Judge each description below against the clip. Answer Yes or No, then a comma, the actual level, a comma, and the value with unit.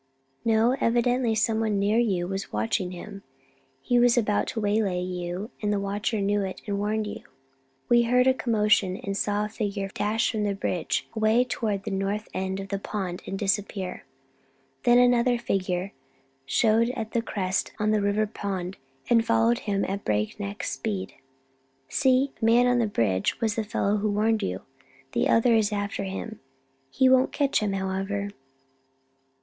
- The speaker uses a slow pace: No, average, 170 wpm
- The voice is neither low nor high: No, high, 210 Hz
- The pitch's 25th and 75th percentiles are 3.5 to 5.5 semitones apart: No, average, 2.7 semitones